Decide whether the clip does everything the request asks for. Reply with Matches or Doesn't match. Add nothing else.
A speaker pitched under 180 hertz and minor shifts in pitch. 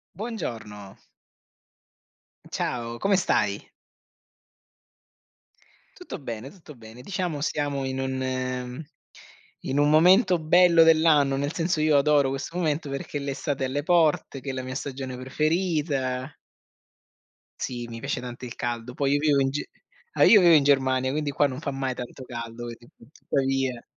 Doesn't match